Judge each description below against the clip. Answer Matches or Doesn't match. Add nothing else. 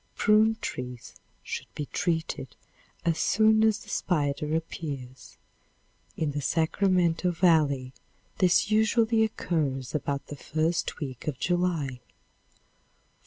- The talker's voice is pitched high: Doesn't match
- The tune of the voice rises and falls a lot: Doesn't match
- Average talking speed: Doesn't match